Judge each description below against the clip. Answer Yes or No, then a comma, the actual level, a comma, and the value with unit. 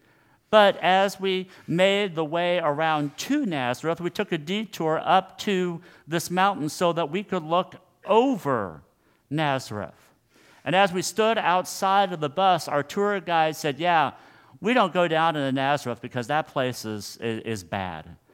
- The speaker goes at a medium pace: Yes, average, 160 wpm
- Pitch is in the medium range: Yes, medium, 170 Hz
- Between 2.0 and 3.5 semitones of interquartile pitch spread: No, average, 5.0 semitones